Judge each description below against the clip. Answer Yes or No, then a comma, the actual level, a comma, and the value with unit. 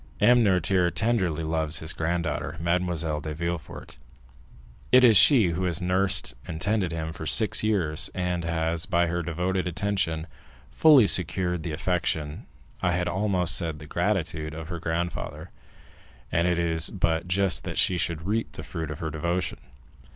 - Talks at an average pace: Yes, average, 160 wpm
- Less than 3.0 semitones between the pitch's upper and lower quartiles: Yes, narrow, 2.4 semitones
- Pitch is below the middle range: Yes, very low, 85 Hz